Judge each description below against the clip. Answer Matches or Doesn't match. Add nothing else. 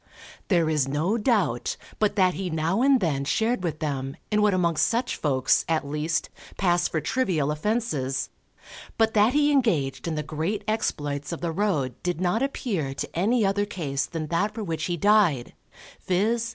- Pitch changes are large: Matches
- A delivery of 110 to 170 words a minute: Doesn't match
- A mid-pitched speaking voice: Matches